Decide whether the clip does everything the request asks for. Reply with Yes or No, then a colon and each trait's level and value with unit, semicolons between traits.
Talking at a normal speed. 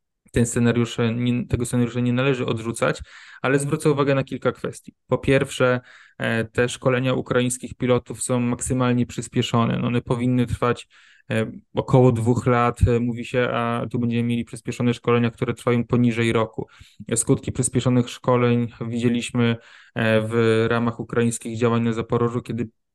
Yes: average, 130 wpm